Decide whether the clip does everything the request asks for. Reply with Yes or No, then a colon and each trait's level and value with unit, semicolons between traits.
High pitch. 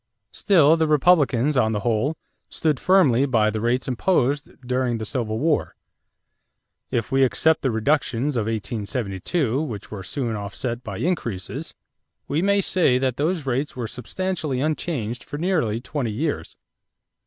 No: low, 130 Hz